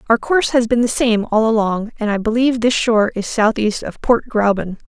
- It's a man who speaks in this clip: No, female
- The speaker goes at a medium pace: No, fast, 220 wpm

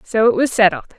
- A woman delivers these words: Yes, female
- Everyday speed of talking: No, fast, 245 wpm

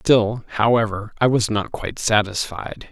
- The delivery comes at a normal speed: Yes, average, 145 wpm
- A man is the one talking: Yes, male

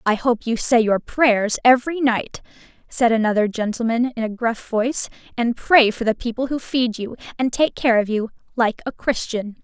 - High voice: Yes, high, 235 Hz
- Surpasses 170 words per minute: Yes, average, 185 wpm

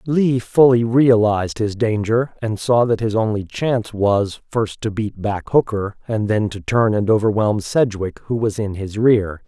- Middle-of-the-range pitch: No, low, 110 Hz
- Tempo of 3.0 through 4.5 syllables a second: Yes, 4.3 syllables/s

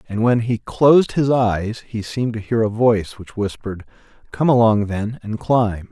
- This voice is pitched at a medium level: No, low, 115 Hz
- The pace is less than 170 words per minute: No, average, 195 wpm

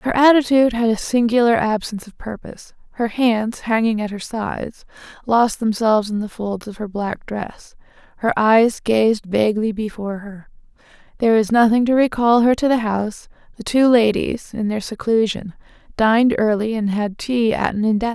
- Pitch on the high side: Yes, high, 220 Hz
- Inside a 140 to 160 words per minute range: No, average, 175 wpm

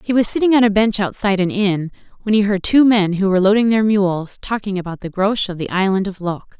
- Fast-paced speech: Yes, fast, 255 wpm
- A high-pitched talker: Yes, high, 200 Hz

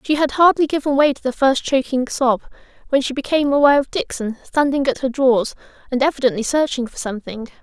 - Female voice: Yes, female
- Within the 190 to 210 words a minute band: Yes, average, 195 wpm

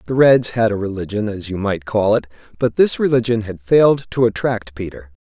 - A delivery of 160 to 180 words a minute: No, fast, 205 wpm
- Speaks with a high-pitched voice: No, low, 110 Hz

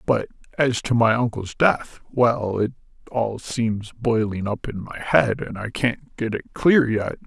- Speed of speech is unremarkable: Yes, average, 175 wpm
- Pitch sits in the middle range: No, low, 115 Hz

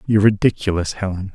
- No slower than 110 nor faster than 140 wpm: Yes, slow, 135 wpm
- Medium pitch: No, low, 100 Hz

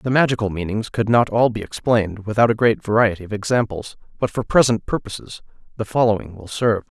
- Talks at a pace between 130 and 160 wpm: No, average, 190 wpm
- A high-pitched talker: No, low, 110 Hz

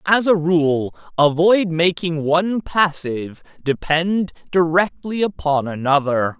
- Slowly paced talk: Yes, slow, 105 wpm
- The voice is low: No, medium, 165 Hz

